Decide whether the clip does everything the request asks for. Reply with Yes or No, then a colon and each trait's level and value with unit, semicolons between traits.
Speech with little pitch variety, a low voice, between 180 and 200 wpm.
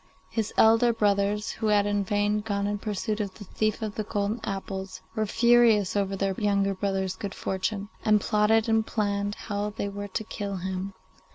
No: narrow, 1.4 semitones; high, 205 Hz; average, 185 wpm